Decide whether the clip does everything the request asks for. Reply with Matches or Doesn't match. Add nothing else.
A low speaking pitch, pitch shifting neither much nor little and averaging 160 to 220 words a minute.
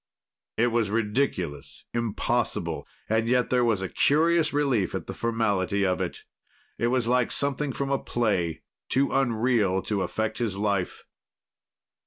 Doesn't match